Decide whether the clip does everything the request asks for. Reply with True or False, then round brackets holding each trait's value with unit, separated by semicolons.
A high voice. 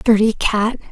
True (220 Hz)